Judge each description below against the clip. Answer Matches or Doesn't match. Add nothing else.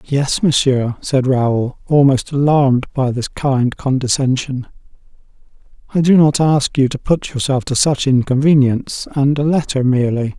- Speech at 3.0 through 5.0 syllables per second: Matches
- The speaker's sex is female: Doesn't match